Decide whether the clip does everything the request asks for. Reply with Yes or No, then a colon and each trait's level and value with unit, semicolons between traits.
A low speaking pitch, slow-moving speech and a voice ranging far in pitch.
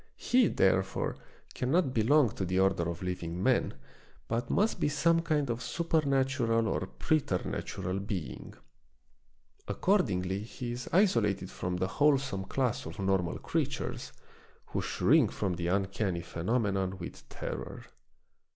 Yes: low, 105 Hz; slow, 125 wpm; wide, 6.5 semitones